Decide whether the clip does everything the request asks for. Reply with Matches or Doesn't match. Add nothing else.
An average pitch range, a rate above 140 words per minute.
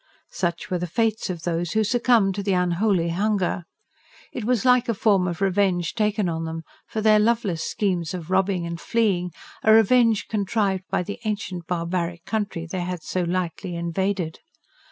Matches